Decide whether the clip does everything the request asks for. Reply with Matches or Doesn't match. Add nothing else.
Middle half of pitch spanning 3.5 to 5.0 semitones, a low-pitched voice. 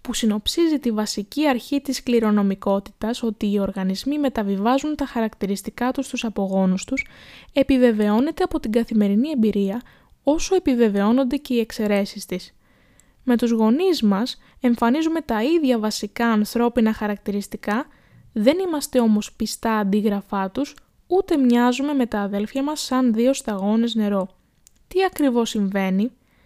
Doesn't match